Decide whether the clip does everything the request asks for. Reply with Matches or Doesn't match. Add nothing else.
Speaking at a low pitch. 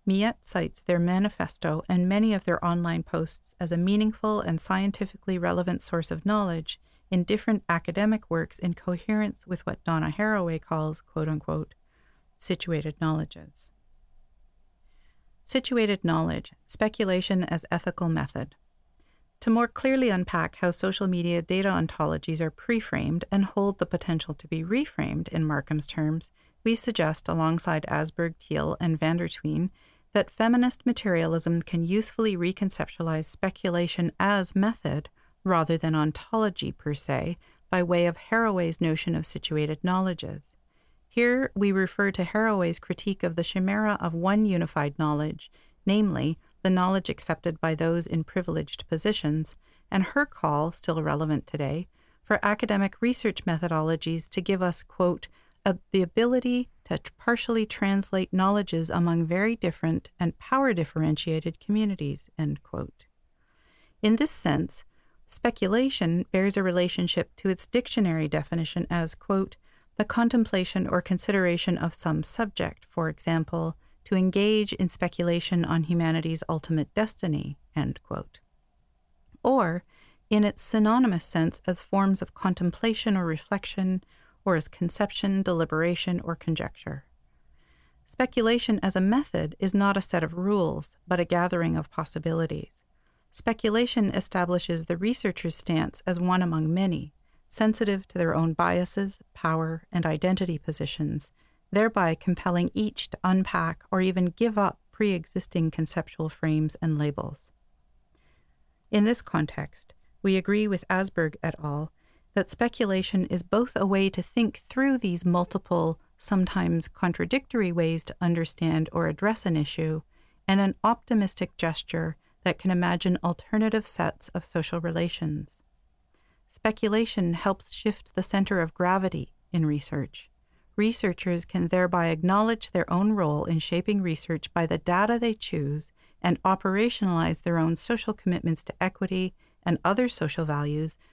Doesn't match